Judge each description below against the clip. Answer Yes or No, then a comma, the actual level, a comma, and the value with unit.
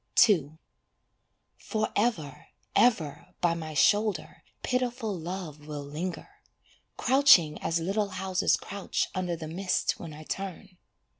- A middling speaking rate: No, slow, 115 wpm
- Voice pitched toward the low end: No, medium, 180 Hz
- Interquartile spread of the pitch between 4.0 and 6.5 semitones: Yes, average, 4.8 semitones